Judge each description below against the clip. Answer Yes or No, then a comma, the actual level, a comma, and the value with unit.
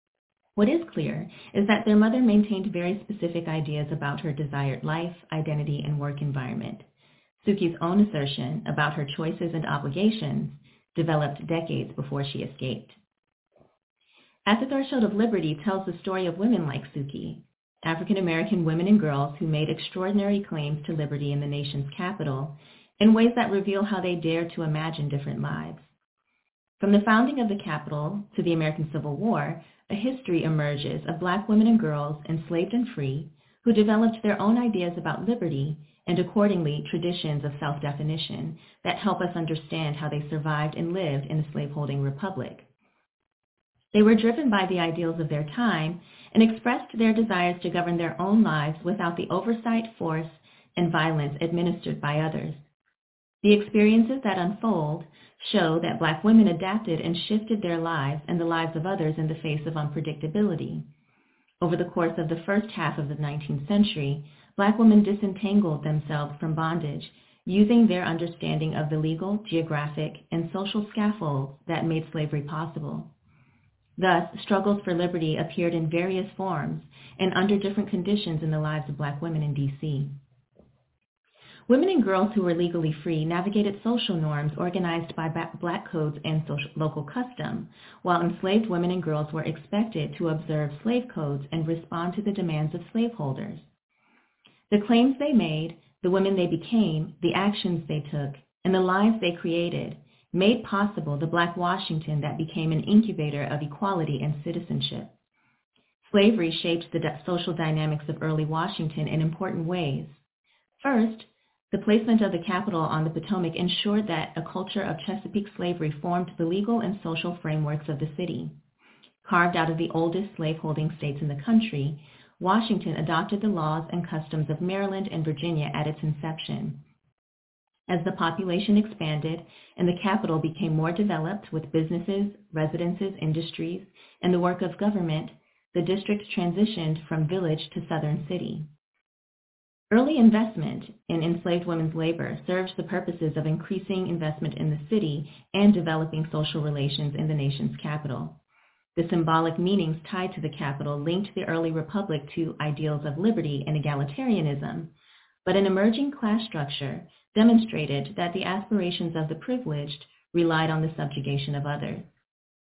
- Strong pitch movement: No, average, 4.1 semitones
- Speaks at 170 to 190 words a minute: No, average, 160 wpm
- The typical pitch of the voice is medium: Yes, medium, 170 Hz